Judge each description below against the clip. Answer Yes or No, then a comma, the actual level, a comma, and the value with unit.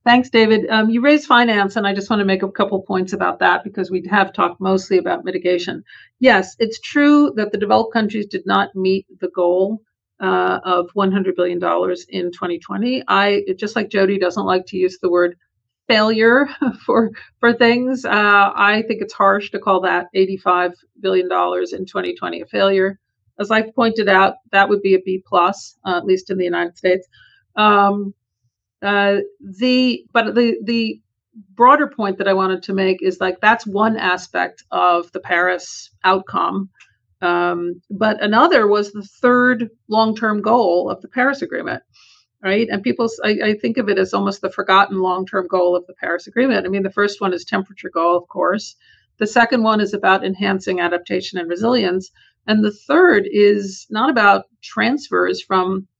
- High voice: Yes, high, 195 Hz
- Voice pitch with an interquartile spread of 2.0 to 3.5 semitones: Yes, average, 3.1 semitones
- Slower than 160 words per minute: No, average, 180 wpm